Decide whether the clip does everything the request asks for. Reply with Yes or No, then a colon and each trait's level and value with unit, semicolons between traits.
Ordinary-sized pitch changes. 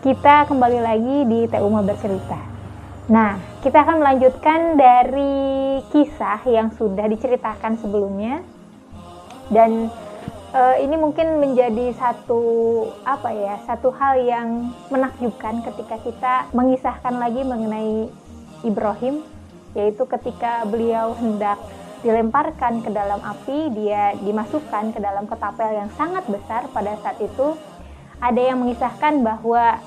Yes: average, 3.2 semitones